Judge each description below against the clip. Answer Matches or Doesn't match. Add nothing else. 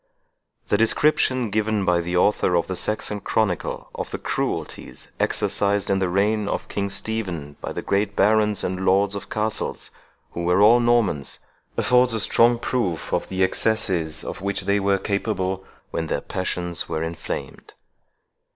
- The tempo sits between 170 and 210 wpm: Doesn't match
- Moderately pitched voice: Doesn't match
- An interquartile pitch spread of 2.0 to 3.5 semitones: Matches